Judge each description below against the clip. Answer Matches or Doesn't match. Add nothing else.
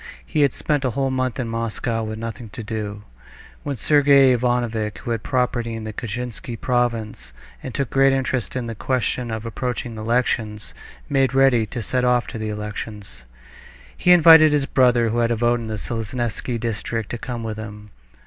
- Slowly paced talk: Doesn't match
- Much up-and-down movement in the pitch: Doesn't match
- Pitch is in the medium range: Doesn't match